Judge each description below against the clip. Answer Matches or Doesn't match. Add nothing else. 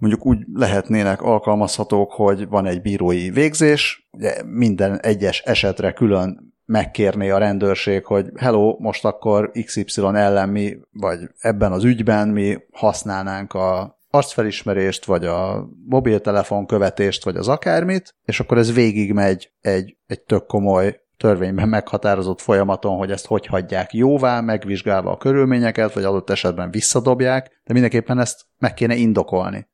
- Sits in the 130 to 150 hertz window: Doesn't match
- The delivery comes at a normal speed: Matches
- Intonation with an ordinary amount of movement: Matches